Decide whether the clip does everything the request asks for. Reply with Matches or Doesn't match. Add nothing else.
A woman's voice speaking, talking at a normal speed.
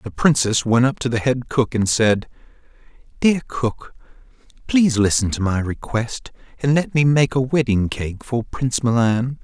Doesn't match